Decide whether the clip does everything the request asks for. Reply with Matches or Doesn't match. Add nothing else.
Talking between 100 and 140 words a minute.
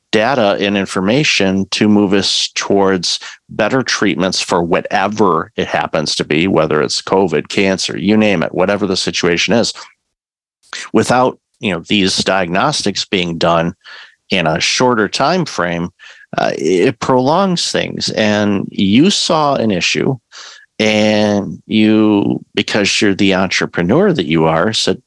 Matches